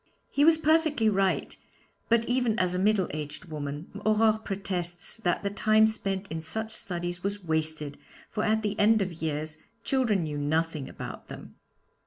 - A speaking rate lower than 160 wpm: No, average, 165 wpm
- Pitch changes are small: No, average, 5.2 semitones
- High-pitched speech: Yes, high, 195 Hz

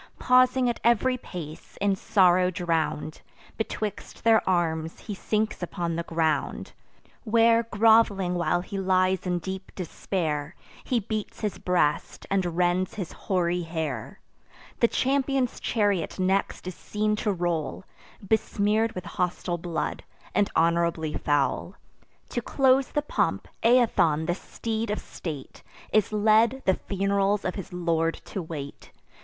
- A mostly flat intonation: No, average, 4.2 semitones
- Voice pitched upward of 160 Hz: Yes, high, 190 Hz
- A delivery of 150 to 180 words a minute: No, slow, 135 wpm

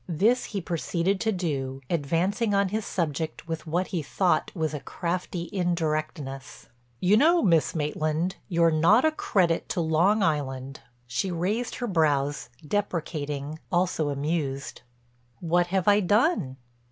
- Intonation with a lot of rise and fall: No, average, 4.1 semitones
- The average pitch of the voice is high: No, medium, 170 Hz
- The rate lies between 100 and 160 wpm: Yes, average, 140 wpm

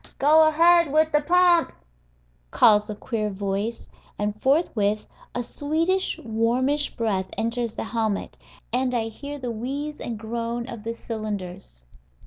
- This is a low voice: No, high, 235 Hz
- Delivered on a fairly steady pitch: No, average, 5.2 semitones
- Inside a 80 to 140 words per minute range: Yes, slow, 135 wpm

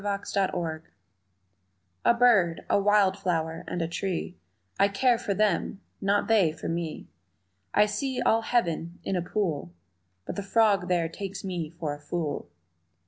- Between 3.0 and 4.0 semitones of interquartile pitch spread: Yes, average, 3.7 semitones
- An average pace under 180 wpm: Yes, average, 150 wpm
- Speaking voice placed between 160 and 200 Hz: Yes, high, 190 Hz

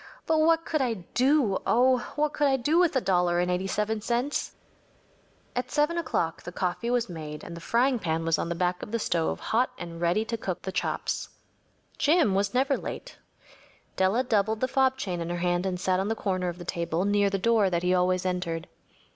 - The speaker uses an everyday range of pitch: No, wide, 6.0 semitones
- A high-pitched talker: Yes, high, 200 Hz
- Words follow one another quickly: Yes, fast, 215 wpm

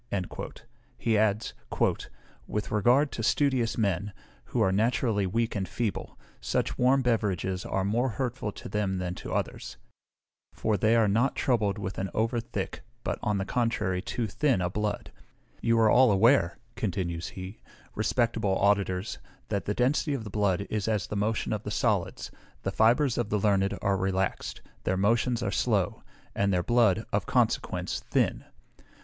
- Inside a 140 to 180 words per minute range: Yes, average, 165 wpm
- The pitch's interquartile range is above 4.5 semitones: No, average, 3.2 semitones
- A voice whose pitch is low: Yes, low, 105 Hz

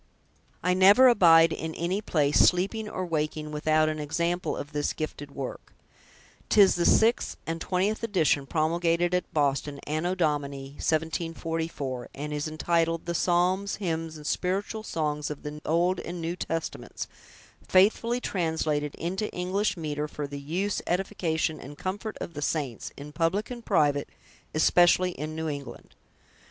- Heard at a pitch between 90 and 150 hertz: No, medium, 165 Hz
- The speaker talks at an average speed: Yes, average, 145 wpm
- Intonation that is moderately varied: Yes, average, 3.3 semitones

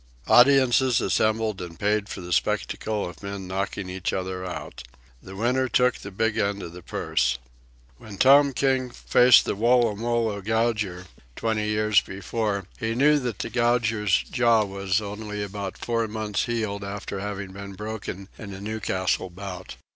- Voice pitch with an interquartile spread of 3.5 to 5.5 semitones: No, average, 2.9 semitones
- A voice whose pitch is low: Yes, low, 105 Hz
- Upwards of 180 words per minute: No, average, 155 wpm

